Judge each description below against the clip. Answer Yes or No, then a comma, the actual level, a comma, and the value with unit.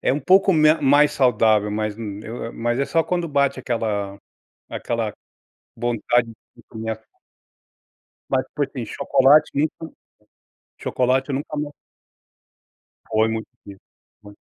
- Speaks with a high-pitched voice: No, low, 125 Hz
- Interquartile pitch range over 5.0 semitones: No, average, 4.7 semitones